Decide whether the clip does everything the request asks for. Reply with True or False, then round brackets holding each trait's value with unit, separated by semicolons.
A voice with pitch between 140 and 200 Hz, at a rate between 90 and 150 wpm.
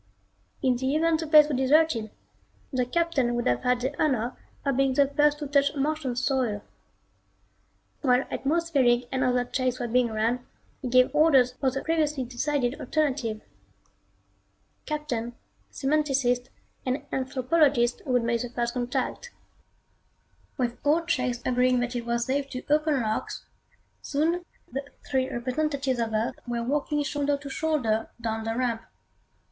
False (260 Hz; 145 wpm)